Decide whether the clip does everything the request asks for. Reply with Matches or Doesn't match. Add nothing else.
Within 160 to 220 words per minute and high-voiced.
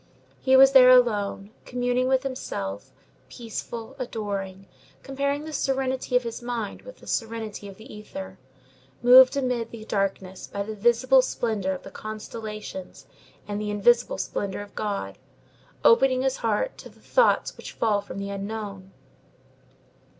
Doesn't match